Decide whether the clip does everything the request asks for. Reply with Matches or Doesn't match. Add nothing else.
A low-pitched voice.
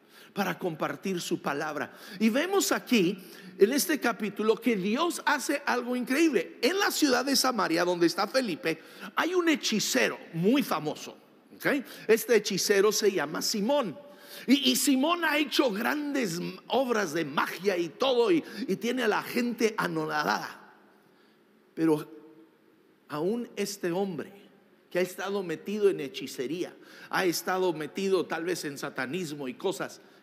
Doesn't match